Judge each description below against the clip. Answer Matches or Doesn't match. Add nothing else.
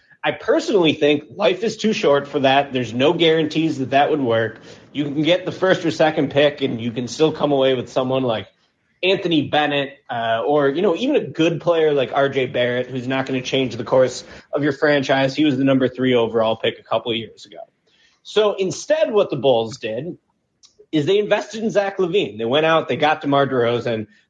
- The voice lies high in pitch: Doesn't match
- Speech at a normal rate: Doesn't match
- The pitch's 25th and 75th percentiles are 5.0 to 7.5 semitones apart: Doesn't match